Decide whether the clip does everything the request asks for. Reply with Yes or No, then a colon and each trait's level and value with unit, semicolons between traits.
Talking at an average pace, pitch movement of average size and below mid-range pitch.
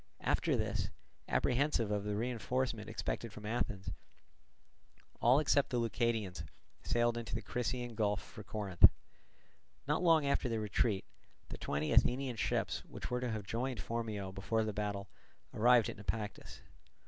Yes: average, 145 wpm; average, 3.0 semitones; low, 115 Hz